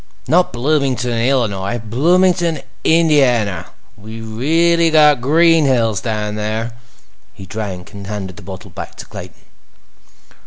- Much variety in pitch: Yes, wide, 6.6 semitones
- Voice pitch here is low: Yes, low, 120 Hz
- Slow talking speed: Yes, slow, 115 wpm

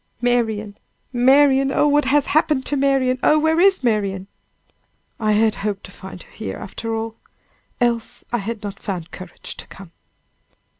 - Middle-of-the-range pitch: No, high, 235 Hz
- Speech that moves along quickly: No, average, 160 wpm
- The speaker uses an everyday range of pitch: Yes, average, 4.9 semitones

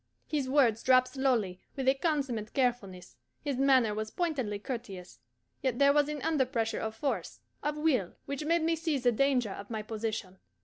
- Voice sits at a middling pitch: No, very high, 255 Hz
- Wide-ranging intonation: No, average, 4.5 semitones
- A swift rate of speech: No, average, 175 wpm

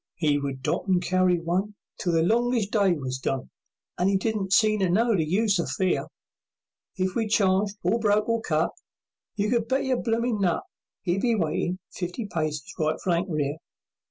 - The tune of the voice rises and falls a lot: No, average, 4.2 semitones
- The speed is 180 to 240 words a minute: Yes, average, 185 wpm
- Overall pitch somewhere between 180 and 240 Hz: Yes, high, 190 Hz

